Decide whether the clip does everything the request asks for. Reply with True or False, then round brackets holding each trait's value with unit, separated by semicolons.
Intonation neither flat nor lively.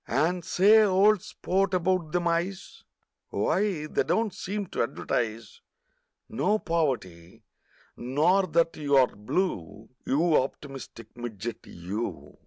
False (7.7 semitones)